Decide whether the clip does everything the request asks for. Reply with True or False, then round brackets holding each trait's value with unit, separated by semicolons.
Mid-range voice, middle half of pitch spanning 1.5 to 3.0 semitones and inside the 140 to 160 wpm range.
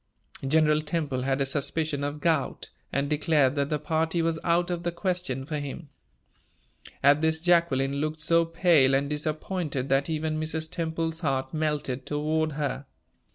True (155 Hz; 2.5 semitones; 155 wpm)